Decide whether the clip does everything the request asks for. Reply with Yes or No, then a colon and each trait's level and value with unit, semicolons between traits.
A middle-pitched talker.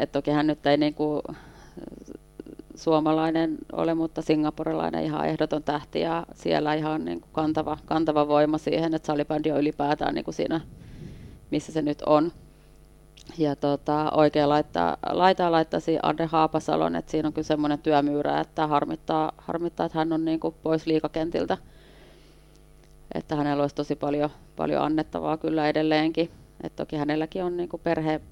Yes: medium, 155 Hz